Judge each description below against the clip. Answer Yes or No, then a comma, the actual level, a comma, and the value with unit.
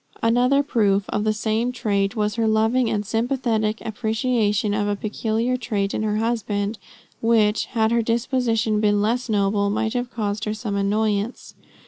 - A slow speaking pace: No, average, 160 wpm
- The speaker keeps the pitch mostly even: Yes, narrow, 2.0 semitones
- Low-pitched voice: No, high, 220 Hz